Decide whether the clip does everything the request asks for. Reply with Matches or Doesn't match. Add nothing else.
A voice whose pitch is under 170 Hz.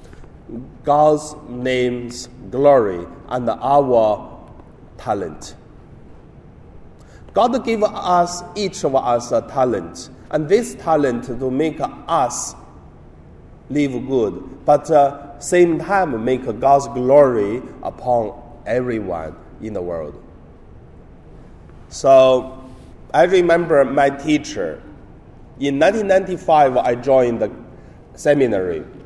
Matches